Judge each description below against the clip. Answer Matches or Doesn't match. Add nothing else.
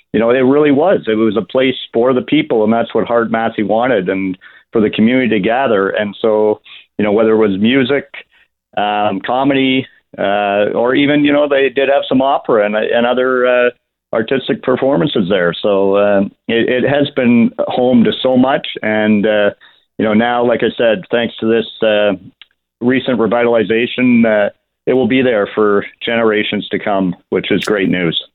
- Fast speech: Doesn't match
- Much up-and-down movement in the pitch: Doesn't match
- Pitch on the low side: Matches